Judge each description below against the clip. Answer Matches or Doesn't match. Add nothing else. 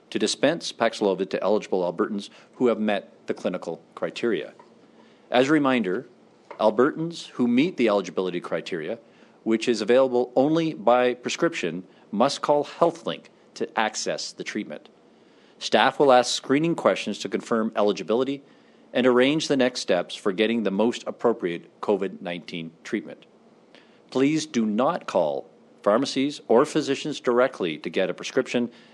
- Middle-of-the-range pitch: Doesn't match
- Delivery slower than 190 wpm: Matches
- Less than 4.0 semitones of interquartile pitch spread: Doesn't match